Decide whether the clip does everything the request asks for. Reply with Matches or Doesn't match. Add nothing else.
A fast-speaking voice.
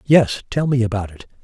Matches